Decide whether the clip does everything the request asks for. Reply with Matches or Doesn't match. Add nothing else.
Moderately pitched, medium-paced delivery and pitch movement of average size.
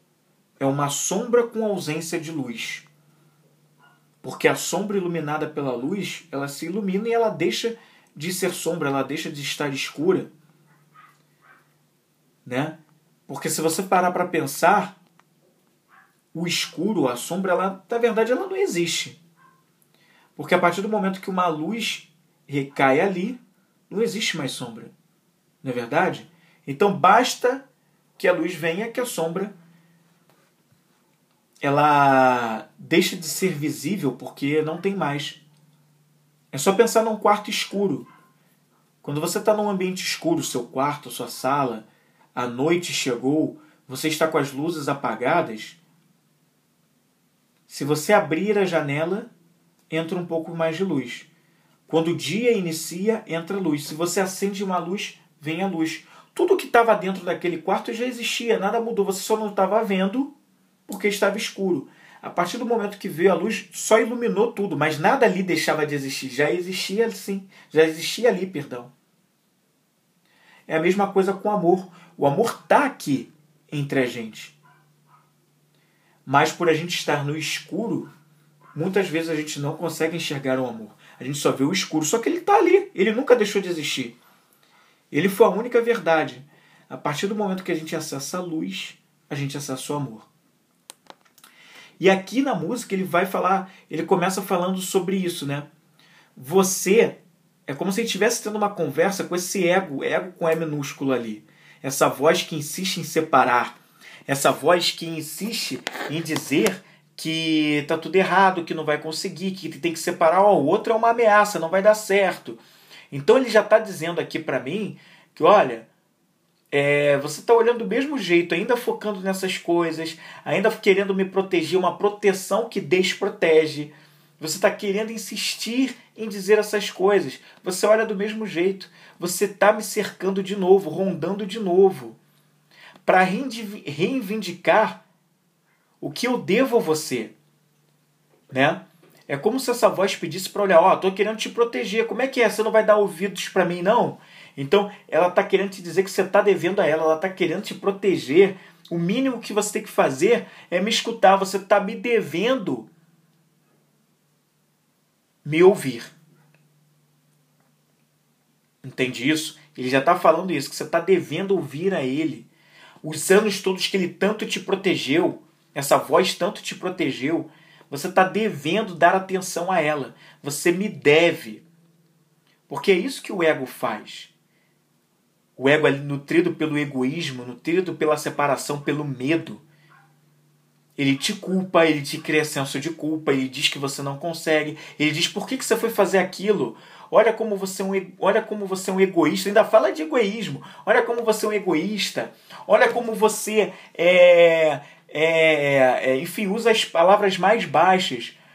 Matches